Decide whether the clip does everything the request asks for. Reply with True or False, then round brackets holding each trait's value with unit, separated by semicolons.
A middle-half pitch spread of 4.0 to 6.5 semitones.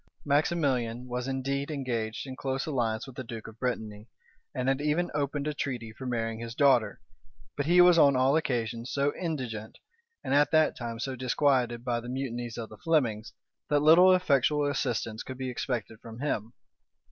False (3.6 semitones)